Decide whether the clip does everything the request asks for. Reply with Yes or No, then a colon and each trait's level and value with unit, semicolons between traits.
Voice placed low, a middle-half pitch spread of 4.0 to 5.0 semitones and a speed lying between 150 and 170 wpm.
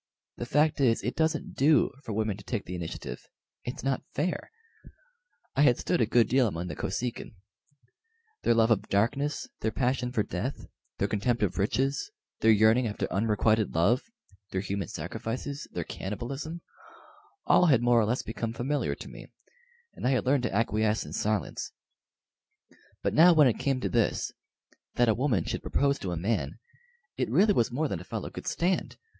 No: low, 115 Hz; average, 4.5 semitones; average, 180 wpm